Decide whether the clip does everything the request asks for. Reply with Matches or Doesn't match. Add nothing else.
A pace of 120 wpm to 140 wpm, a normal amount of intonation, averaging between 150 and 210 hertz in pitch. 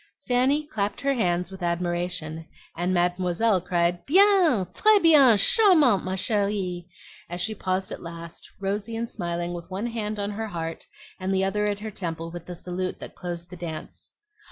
Doesn't match